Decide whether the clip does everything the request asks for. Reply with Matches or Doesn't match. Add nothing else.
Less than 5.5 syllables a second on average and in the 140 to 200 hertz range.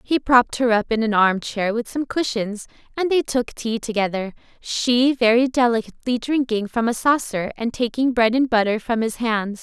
Doesn't match